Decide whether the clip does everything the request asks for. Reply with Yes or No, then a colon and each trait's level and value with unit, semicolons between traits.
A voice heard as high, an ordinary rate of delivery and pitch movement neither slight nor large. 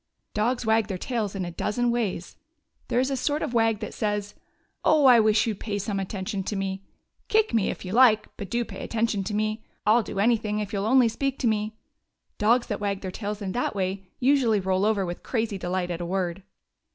No: high, 210 Hz; fast, 235 wpm; average, 3.1 semitones